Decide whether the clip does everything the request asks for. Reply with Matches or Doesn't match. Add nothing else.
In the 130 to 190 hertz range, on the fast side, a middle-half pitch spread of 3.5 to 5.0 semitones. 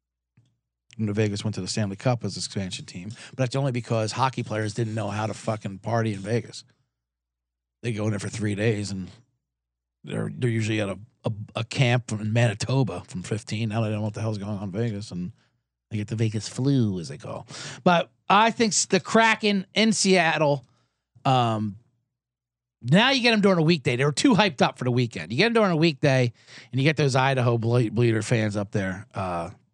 Doesn't match